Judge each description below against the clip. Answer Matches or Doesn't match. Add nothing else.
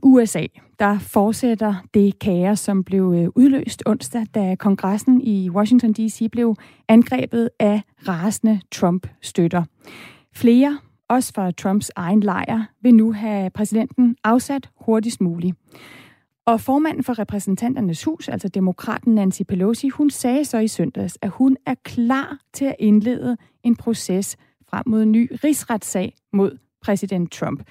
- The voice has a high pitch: Matches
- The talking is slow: Matches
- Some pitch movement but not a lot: Matches